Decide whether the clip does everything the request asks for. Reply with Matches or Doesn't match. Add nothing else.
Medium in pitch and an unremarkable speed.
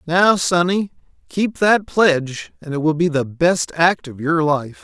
Matches